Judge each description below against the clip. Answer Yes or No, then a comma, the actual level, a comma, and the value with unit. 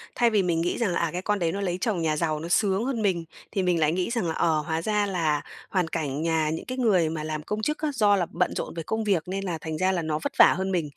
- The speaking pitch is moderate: Yes, medium, 180 Hz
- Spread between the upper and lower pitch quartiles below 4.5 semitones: Yes, average, 4.0 semitones